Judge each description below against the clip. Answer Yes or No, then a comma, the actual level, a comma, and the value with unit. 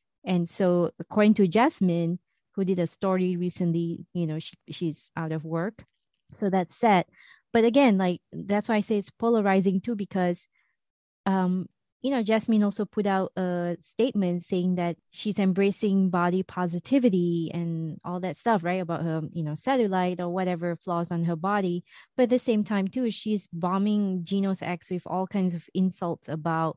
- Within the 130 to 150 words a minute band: No, average, 175 wpm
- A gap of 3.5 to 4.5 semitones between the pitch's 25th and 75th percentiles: No, average, 3.0 semitones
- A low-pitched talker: No, medium, 185 Hz